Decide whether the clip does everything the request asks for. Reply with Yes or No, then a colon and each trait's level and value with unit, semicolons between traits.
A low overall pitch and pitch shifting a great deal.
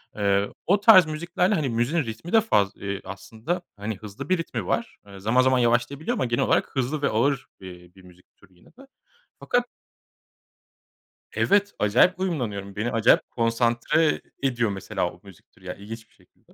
Yes: low, 120 Hz; wide, 7.5 semitones